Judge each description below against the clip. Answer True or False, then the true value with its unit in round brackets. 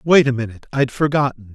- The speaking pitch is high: False (130 Hz)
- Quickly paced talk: False (195 wpm)